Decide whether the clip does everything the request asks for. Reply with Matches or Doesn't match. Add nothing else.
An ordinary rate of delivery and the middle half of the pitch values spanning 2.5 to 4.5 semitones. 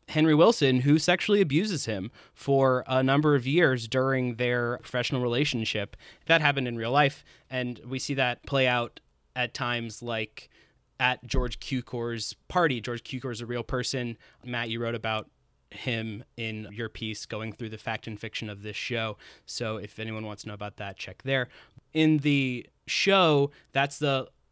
Matches